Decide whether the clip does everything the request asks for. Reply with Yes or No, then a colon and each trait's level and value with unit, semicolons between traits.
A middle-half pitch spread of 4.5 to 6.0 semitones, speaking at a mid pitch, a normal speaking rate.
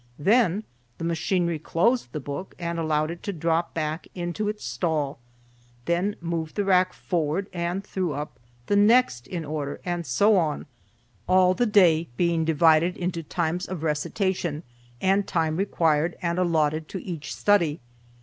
No: average, 3.0 semitones; medium, 170 Hz; average, 160 wpm